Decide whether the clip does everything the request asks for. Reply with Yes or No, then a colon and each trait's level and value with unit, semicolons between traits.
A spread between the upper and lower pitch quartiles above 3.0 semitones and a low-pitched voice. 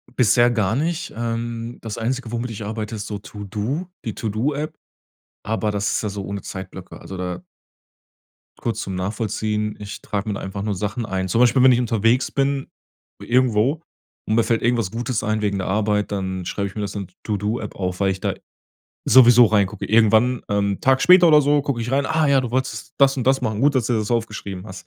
Yes: average, 3.5 semitones; low, 110 Hz